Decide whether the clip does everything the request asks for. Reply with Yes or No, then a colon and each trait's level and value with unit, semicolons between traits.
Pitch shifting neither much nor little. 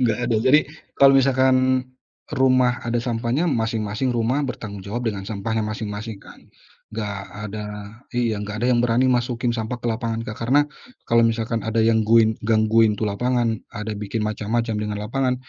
No: narrow, 2.3 semitones